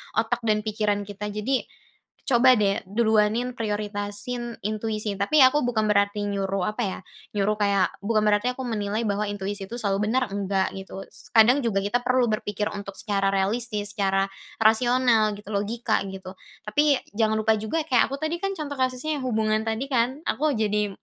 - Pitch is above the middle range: Yes, high, 215 Hz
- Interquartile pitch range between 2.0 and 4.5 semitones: Yes, average, 3.1 semitones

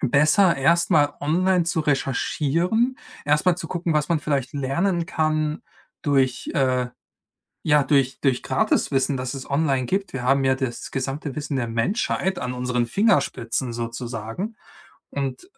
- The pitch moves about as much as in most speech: Yes, average, 4.2 semitones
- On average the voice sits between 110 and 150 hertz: Yes, medium, 140 Hz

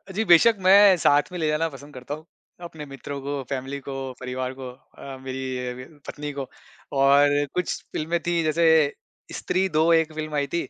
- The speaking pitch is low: No, medium, 145 Hz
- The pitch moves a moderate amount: Yes, average, 3.3 semitones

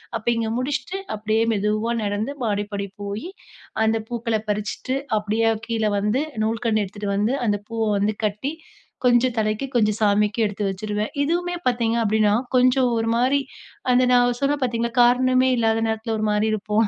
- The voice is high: Yes, high, 225 Hz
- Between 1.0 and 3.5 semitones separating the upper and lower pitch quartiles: Yes, average, 2.7 semitones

